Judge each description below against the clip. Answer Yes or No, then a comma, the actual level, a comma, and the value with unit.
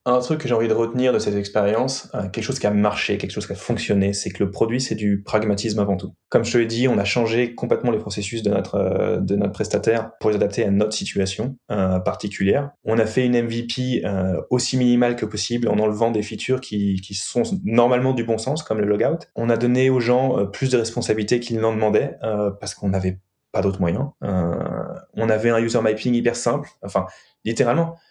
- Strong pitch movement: No, average, 3.2 semitones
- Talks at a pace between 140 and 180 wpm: No, fast, 220 wpm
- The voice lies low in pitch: Yes, low, 110 Hz